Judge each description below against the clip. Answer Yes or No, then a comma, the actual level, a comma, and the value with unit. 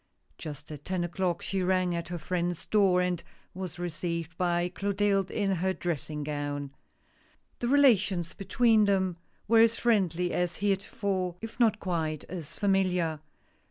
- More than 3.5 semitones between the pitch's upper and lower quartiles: No, narrow, 2.6 semitones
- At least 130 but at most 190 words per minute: Yes, average, 145 wpm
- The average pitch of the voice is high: No, medium, 180 Hz